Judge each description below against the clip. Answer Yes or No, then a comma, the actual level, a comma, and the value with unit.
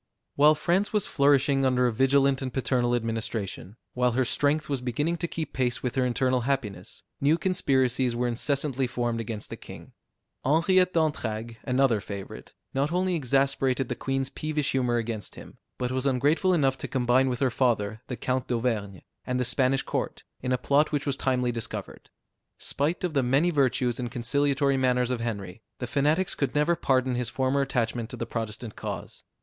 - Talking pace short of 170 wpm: No, average, 180 wpm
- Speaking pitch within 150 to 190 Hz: No, low, 130 Hz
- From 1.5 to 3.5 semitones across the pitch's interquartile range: Yes, average, 2.8 semitones